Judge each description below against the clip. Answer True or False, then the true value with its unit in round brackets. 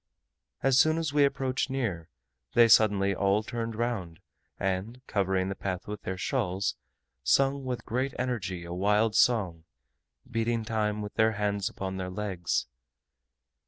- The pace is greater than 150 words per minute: False (145 wpm)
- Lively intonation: False (4.1 semitones)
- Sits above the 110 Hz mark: False (105 Hz)